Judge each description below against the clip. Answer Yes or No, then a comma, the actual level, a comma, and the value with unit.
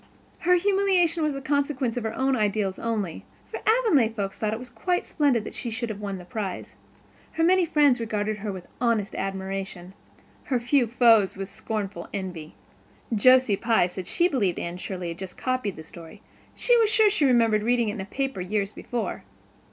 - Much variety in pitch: Yes, wide, 5.7 semitones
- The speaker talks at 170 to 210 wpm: Yes, average, 190 wpm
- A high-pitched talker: Yes, high, 225 Hz